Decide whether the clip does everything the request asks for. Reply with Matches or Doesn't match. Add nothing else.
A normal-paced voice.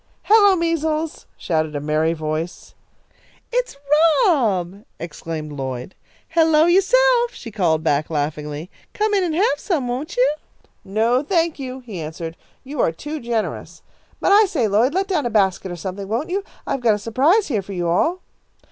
Matches